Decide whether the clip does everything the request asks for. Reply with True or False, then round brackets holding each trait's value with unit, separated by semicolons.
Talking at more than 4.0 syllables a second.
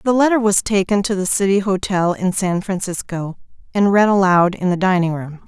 True (5.3 syllables/s)